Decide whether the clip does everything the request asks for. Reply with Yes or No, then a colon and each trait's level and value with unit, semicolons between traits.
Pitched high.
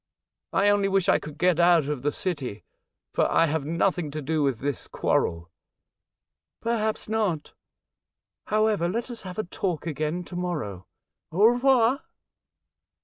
No: medium, 175 Hz